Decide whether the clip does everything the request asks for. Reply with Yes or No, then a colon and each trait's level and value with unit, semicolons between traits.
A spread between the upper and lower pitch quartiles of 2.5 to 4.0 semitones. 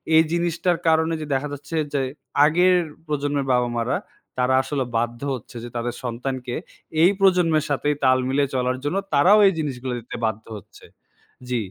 No: average, 4.6 semitones